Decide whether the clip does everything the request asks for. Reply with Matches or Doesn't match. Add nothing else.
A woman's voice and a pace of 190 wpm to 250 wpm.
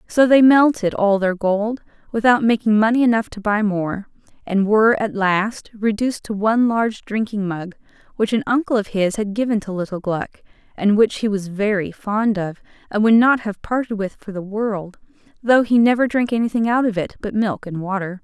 Matches